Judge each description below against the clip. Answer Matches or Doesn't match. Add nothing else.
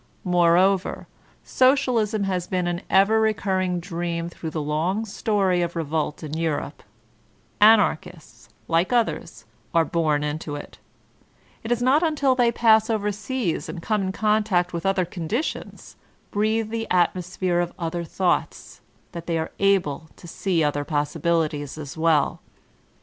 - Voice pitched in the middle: Matches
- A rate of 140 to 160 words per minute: Matches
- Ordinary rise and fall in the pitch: Matches